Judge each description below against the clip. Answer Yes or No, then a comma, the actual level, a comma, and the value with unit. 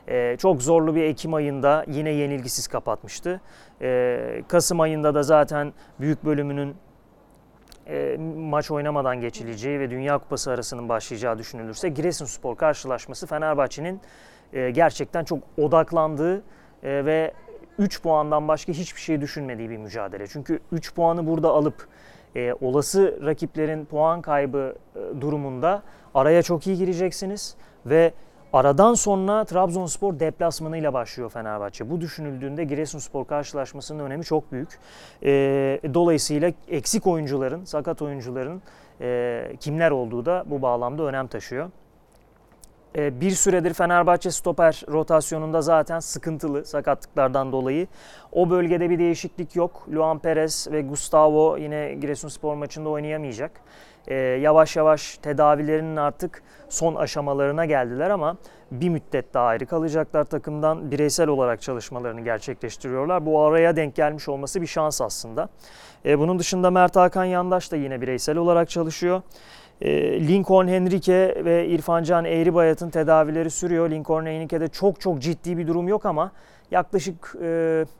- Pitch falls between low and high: Yes, medium, 155 Hz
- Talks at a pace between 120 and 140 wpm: Yes, average, 125 wpm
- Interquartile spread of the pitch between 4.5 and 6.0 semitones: No, average, 3.2 semitones